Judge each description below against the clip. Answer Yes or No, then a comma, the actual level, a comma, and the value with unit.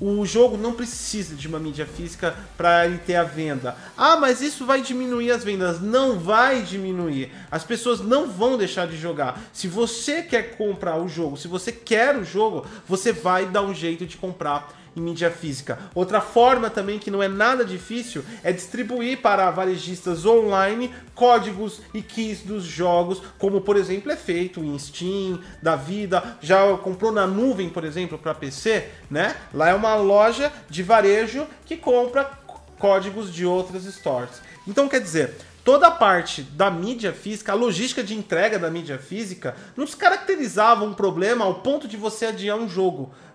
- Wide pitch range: No, average, 4.8 semitones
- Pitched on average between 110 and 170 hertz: No, high, 200 Hz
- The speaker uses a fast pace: No, average, 175 wpm